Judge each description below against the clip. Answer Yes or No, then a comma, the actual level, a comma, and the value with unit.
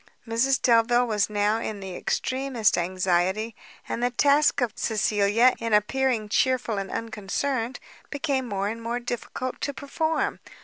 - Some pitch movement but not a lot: Yes, average, 3.7 semitones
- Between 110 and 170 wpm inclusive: Yes, average, 140 wpm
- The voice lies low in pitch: No, high, 230 Hz